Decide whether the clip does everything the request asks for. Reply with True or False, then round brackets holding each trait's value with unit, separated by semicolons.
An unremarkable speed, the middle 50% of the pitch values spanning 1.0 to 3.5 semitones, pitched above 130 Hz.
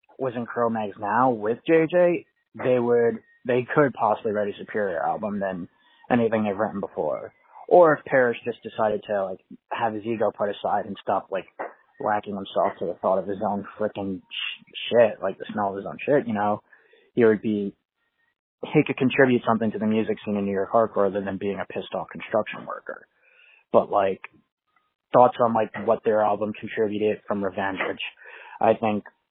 False (190 wpm; 3.2 semitones; 110 Hz)